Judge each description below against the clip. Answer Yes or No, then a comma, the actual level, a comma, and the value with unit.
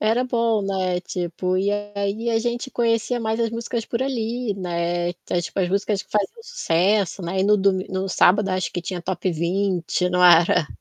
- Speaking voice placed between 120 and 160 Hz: No, high, 195 Hz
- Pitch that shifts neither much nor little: Yes, average, 3.9 semitones